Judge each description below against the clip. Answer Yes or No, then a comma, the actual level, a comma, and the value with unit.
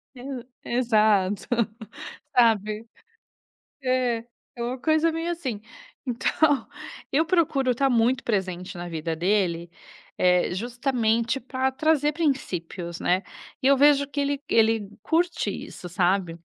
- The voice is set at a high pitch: Yes, high, 240 Hz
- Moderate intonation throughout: No, wide, 5.8 semitones